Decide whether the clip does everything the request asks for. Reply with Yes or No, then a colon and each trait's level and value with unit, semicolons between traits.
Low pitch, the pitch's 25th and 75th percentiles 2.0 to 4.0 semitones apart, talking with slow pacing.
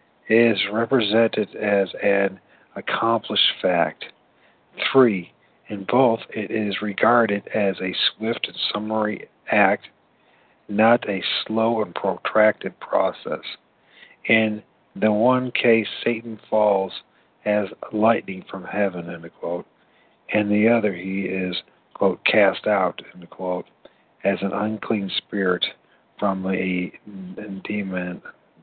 Yes: low, 105 Hz; narrow, 2.6 semitones; slow, 110 wpm